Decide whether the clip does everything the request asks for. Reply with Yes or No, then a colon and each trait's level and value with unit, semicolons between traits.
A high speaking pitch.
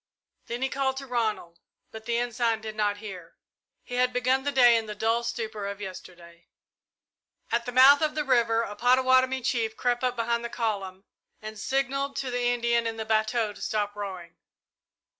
Yes: high, 235 Hz